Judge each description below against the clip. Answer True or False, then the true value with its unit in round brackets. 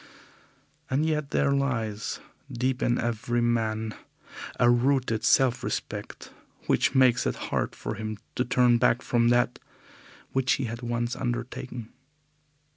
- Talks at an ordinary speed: False (130 wpm)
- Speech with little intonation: True (1.9 semitones)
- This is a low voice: True (120 Hz)